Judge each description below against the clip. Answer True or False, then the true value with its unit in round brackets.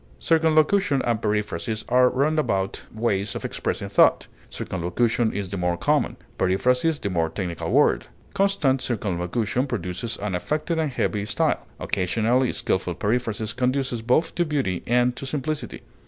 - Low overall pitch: True (120 Hz)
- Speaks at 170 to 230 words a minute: False (140 wpm)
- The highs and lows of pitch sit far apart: True (5.8 semitones)